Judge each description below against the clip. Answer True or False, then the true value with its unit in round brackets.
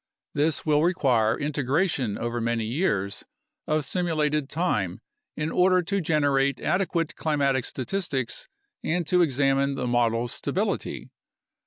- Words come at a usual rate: False (125 wpm)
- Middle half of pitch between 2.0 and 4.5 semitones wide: False (5.2 semitones)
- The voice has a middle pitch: True (145 Hz)